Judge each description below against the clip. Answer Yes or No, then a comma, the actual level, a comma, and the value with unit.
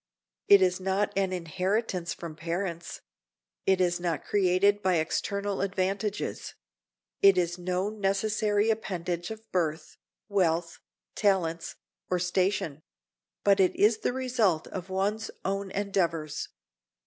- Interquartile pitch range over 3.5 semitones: No, narrow, 2.5 semitones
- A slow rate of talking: Yes, slow, 120 wpm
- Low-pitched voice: No, high, 190 Hz